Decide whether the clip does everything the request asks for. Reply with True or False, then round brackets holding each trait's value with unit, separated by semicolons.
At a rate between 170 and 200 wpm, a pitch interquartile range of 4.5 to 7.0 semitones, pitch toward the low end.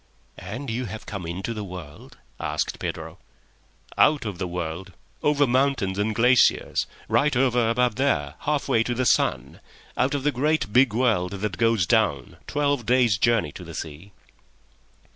False (160 wpm; 5.2 semitones; 115 Hz)